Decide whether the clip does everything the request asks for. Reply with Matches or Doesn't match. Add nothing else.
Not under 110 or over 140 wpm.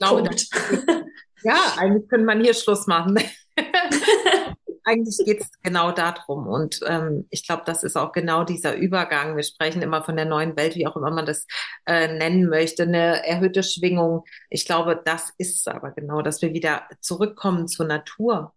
Doesn't match